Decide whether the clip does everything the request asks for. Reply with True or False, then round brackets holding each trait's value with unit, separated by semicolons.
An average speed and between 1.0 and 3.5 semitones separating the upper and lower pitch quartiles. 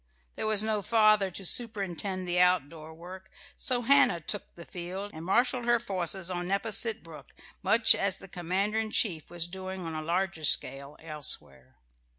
False (165 wpm; 4.0 semitones)